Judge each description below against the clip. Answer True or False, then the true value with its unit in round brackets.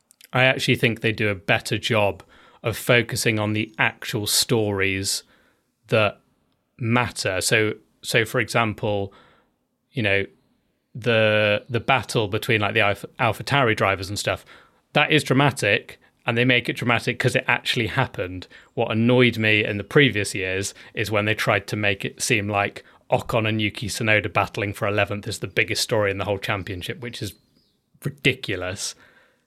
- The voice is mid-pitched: False (110 Hz)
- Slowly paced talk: False (165 wpm)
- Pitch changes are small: False (3.2 semitones)